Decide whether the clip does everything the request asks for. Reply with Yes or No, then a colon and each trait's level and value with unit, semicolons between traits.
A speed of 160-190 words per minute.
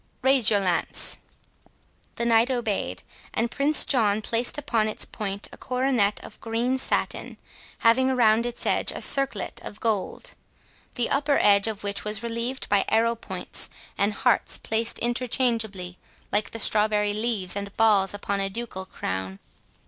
No: average, 150 wpm